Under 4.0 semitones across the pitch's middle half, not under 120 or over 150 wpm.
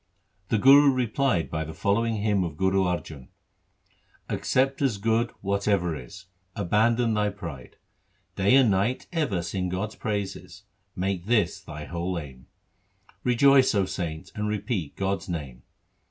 No: average, 4.8 semitones; average, 140 wpm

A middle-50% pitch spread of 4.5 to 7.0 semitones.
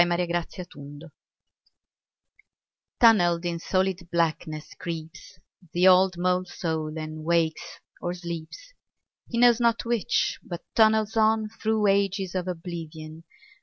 No: average, 4.0 semitones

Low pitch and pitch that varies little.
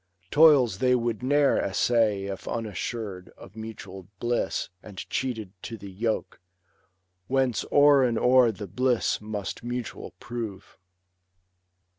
No: low, 115 Hz; average, 3.8 semitones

